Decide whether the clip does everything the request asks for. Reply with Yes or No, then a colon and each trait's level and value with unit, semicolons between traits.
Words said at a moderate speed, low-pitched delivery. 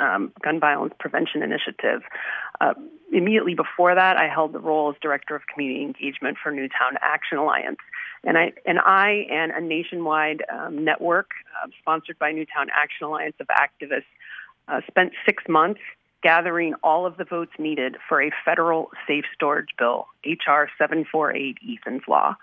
No: average, 160 wpm; medium, 160 Hz